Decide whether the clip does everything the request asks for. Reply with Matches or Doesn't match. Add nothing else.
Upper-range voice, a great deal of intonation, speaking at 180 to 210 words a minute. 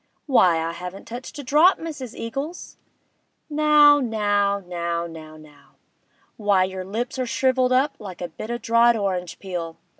Doesn't match